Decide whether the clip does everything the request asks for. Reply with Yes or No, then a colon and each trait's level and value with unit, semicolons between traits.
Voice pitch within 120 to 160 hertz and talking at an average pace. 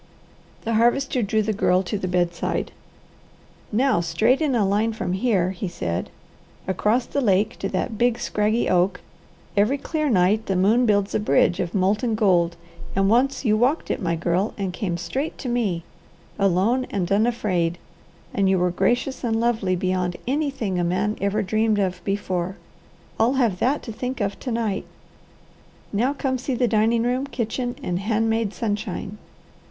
No: high, 210 Hz; average, 170 wpm